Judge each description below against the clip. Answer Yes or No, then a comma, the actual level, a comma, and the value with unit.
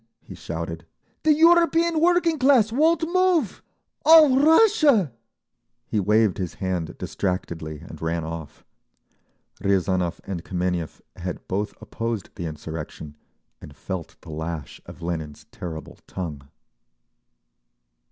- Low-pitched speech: Yes, very low, 95 Hz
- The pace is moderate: No, slow, 115 wpm